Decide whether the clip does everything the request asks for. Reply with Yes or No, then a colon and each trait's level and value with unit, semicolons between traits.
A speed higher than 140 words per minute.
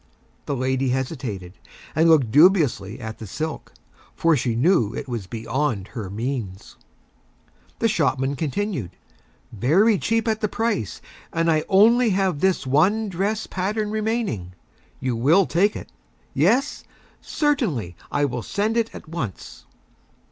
No: slow, 135 wpm